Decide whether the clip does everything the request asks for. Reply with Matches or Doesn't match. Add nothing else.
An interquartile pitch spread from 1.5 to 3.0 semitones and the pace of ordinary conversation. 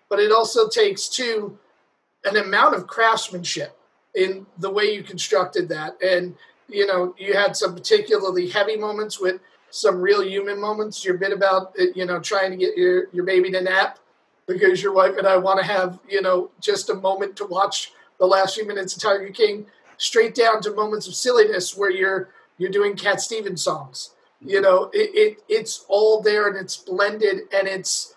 Matches